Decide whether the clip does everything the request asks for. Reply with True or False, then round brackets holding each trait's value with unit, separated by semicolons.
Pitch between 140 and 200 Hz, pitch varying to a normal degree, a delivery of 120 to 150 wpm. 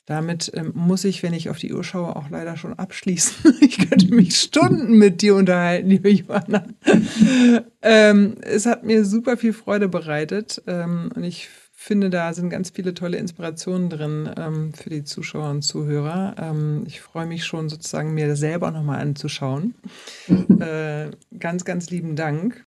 False (185 Hz; 4.5 semitones; 165 wpm)